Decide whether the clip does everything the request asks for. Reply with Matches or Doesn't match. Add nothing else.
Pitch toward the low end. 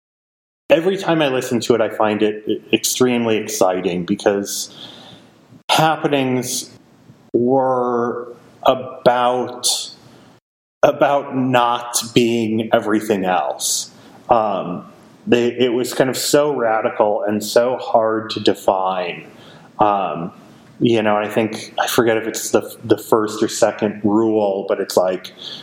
Matches